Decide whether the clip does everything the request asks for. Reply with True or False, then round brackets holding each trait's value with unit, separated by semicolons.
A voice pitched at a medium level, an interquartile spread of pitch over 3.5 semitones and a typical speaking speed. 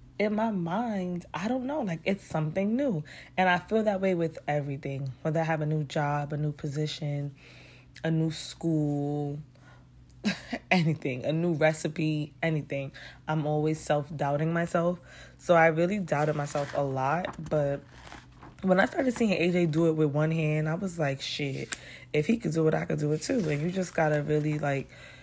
False (155 Hz; 3.0 semitones; 185 wpm)